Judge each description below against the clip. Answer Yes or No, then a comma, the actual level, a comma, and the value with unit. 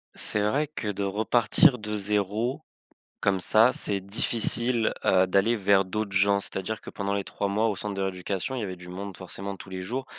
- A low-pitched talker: Yes, low, 100 Hz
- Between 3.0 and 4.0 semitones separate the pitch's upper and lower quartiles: No, narrow, 2.5 semitones